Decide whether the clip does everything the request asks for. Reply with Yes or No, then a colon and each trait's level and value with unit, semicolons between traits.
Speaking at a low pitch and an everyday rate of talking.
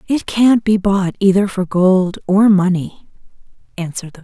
No: high, 190 Hz; average, 170 wpm